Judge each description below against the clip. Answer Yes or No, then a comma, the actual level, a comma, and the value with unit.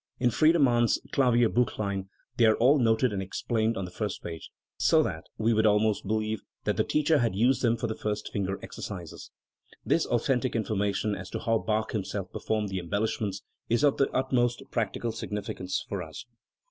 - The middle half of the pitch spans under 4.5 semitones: Yes, average, 3.1 semitones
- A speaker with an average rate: Yes, average, 185 wpm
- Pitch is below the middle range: Yes, low, 110 Hz